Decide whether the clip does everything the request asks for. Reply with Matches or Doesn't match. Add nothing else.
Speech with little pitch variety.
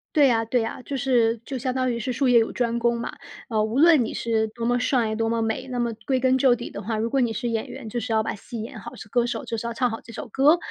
Matches